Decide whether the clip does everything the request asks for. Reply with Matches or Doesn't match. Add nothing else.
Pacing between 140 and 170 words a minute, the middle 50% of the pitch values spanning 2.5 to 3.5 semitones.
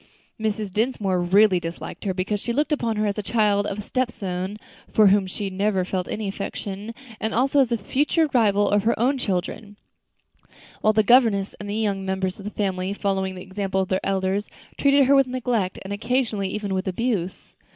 Doesn't match